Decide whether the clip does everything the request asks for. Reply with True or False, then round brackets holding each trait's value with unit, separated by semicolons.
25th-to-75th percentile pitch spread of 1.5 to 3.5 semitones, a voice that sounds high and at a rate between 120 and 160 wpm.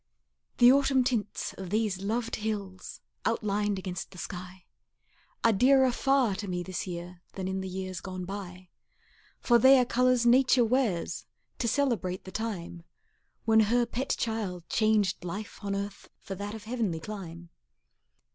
False (4.1 semitones; 205 Hz; 155 wpm)